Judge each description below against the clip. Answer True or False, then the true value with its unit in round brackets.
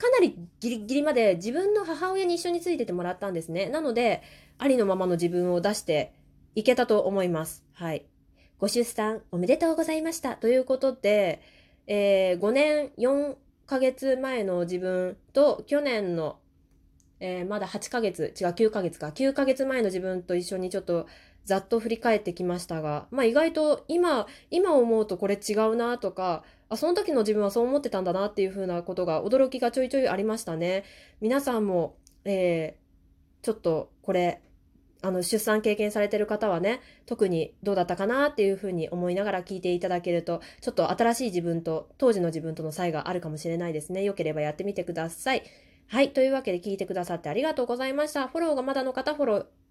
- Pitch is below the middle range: False (205 Hz)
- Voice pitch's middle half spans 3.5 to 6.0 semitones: False (6.5 semitones)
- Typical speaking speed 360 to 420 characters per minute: True (390 characters per minute)